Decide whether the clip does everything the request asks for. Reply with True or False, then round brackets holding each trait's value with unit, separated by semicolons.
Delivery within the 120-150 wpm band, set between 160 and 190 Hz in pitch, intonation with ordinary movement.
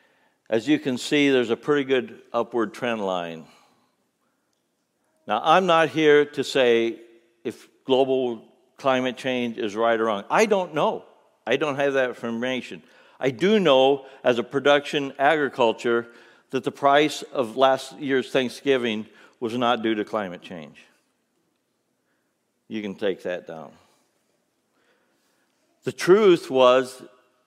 False (135 wpm; 130 Hz; 3.6 semitones)